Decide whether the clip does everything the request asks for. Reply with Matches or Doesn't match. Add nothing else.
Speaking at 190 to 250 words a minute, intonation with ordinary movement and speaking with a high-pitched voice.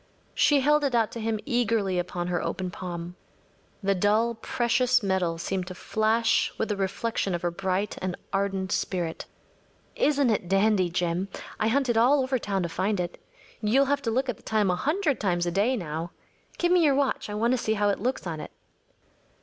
Matches